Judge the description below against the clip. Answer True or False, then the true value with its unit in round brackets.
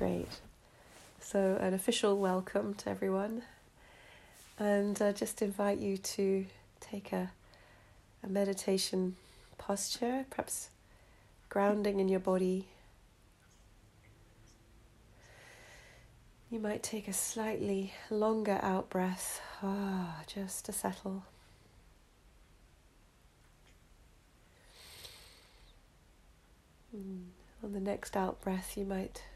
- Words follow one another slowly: True (90 wpm)